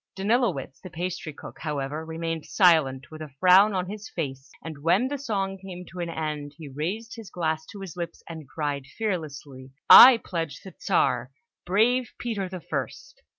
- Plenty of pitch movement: No, average, 4.4 semitones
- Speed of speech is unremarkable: Yes, average, 175 wpm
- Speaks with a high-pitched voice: No, medium, 170 Hz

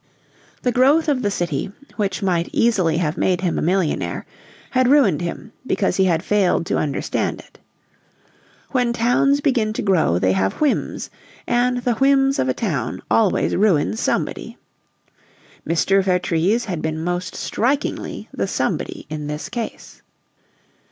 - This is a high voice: Yes, high, 195 Hz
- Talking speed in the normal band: Yes, average, 145 wpm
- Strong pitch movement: Yes, wide, 6.7 semitones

